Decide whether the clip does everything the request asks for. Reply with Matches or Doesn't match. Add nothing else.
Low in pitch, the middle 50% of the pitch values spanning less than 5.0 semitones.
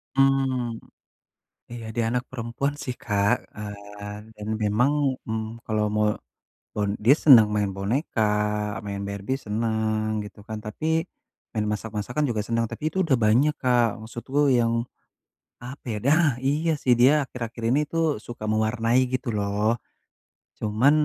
Matches